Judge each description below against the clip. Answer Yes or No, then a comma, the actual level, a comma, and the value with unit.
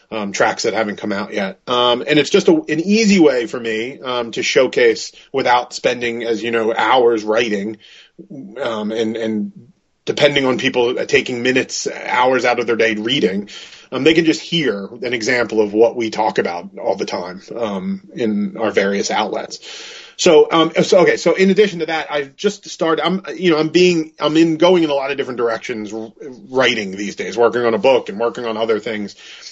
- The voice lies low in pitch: Yes, low, 125 Hz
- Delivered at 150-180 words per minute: No, average, 200 wpm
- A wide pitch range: Yes, wide, 6.4 semitones